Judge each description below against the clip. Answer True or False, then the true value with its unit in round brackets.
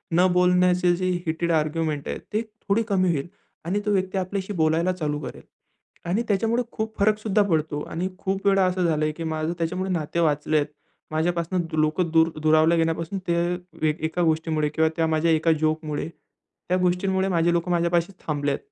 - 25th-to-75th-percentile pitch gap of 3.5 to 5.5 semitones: False (2.9 semitones)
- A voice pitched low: False (170 Hz)